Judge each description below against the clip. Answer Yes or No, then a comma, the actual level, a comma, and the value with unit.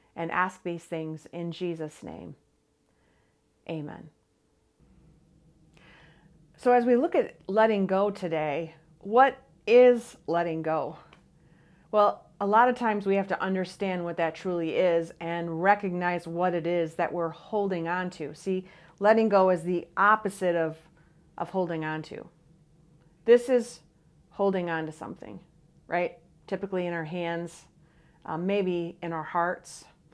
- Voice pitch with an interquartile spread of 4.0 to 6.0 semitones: No, average, 2.9 semitones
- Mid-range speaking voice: Yes, medium, 170 Hz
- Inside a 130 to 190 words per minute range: Yes, average, 140 wpm